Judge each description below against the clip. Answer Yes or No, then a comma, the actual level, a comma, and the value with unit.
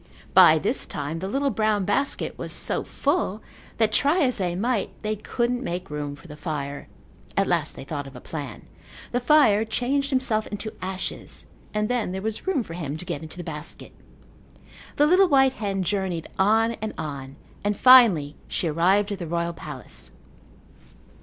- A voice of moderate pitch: No, high, 200 Hz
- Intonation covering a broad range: Yes, wide, 6.6 semitones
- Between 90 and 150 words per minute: No, average, 180 wpm